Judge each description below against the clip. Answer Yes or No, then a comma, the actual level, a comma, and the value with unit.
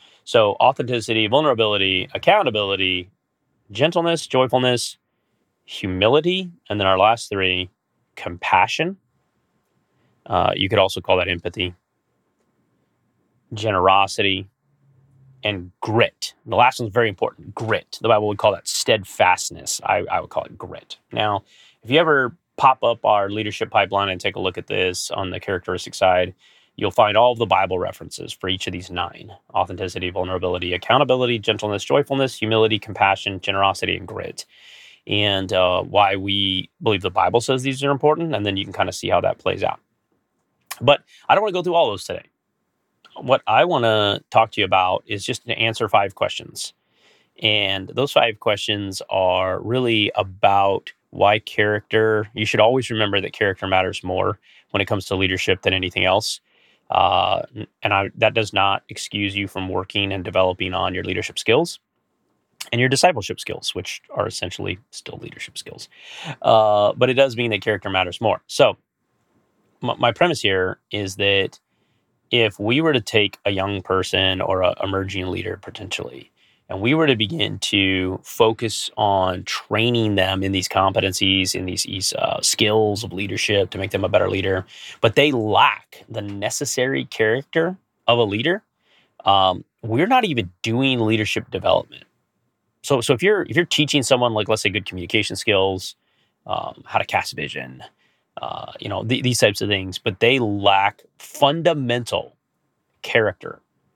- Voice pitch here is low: Yes, low, 100 Hz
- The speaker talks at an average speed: Yes, average, 160 wpm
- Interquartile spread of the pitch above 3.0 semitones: Yes, average, 3.5 semitones